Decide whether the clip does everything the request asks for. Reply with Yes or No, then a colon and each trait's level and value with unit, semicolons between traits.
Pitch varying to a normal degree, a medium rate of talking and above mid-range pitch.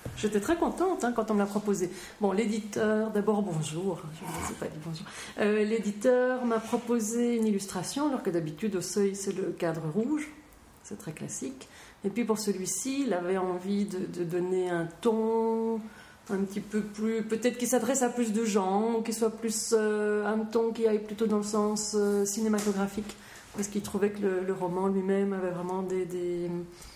Yes: average, 3.0 semitones; average, 195 wpm; high, 210 Hz